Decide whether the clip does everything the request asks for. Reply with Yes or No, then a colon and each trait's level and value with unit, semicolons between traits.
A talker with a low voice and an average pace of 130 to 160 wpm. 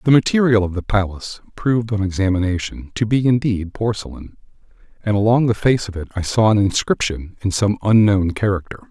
No: low, 105 Hz; average, 175 wpm